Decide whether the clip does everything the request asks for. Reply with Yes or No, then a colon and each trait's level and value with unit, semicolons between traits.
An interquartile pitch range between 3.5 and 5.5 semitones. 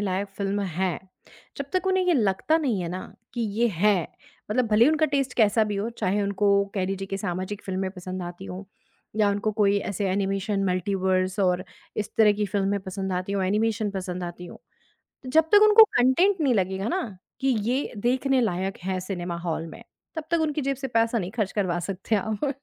Yes: average, 3.8 semitones